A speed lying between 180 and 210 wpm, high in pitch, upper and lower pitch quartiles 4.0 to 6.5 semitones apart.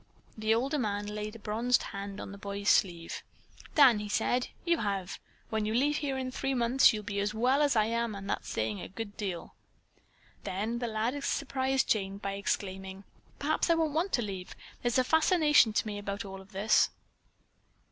Yes: average, 190 wpm; high, 220 Hz; average, 4.5 semitones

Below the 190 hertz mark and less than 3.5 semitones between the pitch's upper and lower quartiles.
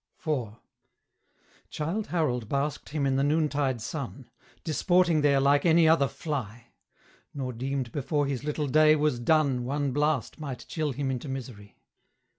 Yes: medium, 140 Hz; average, 2.8 semitones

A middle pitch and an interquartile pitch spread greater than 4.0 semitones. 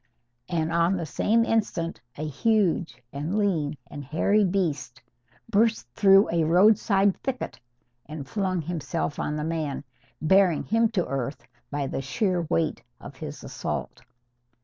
Yes: medium, 170 Hz; average, 4.8 semitones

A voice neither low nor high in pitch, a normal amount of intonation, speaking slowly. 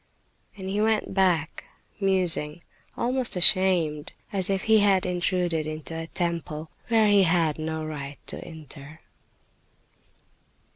Yes: medium, 175 Hz; average, 3.6 semitones; slow, 125 wpm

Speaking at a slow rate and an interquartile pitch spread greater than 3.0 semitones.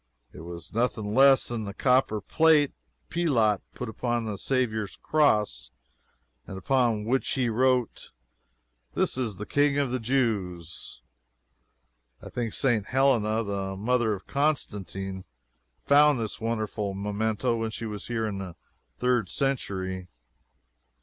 Yes: slow, 130 wpm; average, 4.2 semitones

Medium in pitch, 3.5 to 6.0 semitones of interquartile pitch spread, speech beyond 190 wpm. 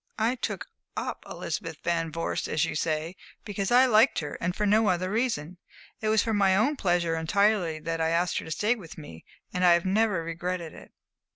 Yes: medium, 180 Hz; average, 4.4 semitones; fast, 205 wpm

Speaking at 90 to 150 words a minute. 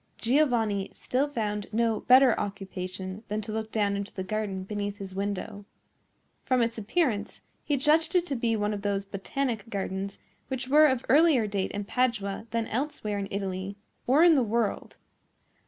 No: average, 170 wpm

